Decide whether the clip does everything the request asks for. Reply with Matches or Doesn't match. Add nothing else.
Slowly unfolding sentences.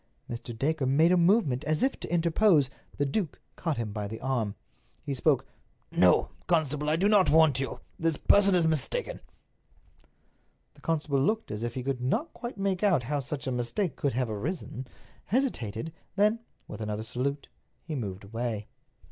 Doesn't match